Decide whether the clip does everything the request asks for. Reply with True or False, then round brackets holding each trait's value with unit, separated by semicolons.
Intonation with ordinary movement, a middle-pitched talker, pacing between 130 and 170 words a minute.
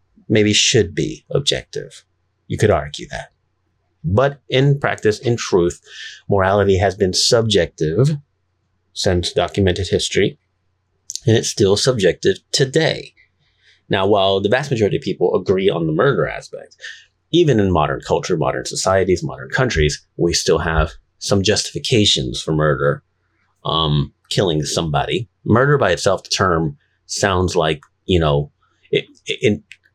False (3.7 semitones; 95 Hz; 135 wpm)